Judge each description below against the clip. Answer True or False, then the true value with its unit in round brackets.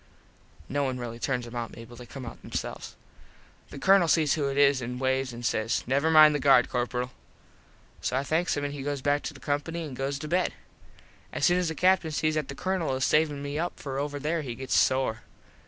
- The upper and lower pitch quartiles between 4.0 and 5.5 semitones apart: False (3.1 semitones)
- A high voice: False (140 Hz)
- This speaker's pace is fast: True (225 wpm)